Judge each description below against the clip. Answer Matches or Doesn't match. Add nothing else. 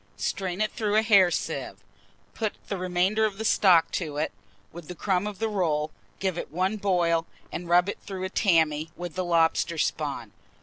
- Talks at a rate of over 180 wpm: Matches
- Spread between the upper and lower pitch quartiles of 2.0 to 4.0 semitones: Matches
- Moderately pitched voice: Matches